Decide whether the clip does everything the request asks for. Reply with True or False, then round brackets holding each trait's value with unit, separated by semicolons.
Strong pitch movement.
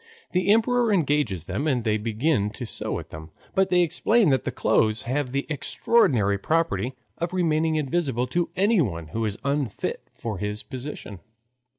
True (7.6 semitones)